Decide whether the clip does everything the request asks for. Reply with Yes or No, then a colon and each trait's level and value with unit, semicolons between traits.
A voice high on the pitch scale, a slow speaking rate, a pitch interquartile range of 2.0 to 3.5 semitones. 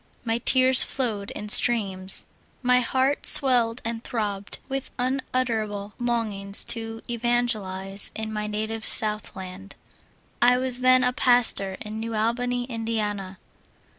Yes: high, 225 Hz; slow, 125 wpm; average, 3.0 semitones